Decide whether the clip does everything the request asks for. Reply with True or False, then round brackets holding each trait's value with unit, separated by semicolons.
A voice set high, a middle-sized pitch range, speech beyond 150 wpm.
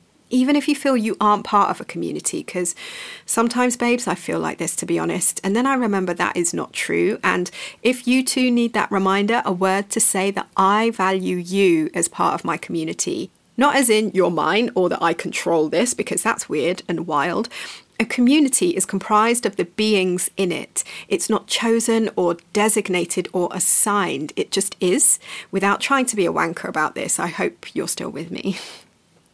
True (205 Hz; 4.6 semitones; 195 wpm)